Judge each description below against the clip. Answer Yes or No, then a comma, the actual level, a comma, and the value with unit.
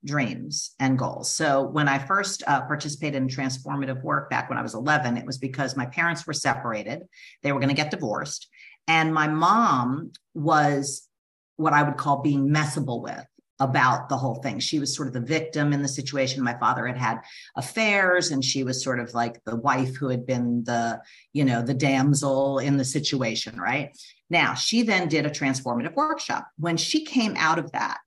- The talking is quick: No, average, 195 wpm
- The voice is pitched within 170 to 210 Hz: No, medium, 140 Hz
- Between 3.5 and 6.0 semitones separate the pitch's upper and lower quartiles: No, narrow, 2.5 semitones